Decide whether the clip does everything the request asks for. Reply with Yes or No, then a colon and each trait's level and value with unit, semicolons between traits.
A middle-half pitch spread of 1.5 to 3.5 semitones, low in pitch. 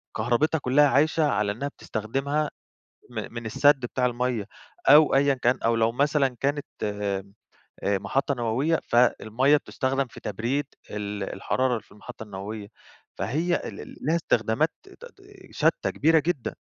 No: average, 4.6 semitones; low, 125 Hz